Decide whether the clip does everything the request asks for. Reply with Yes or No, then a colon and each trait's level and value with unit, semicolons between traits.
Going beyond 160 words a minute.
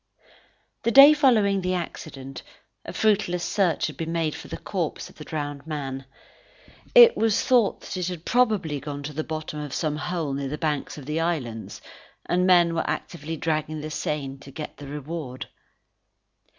Yes: average, 175 wpm